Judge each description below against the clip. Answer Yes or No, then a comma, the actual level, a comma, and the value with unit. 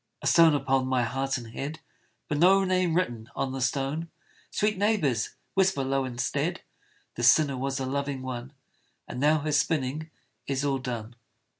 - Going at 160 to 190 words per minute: Yes, average, 165 wpm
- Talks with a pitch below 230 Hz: Yes, low, 135 Hz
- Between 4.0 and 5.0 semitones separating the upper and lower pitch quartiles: No, average, 3.5 semitones